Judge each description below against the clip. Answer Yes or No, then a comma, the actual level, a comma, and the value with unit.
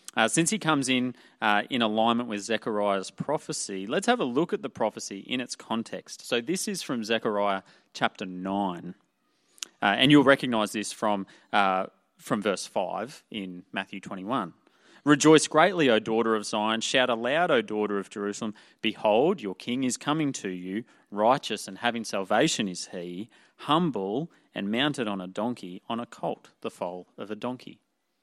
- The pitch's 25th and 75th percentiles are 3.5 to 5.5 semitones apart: Yes, average, 4.1 semitones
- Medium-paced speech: Yes, average, 170 wpm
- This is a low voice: Yes, low, 110 Hz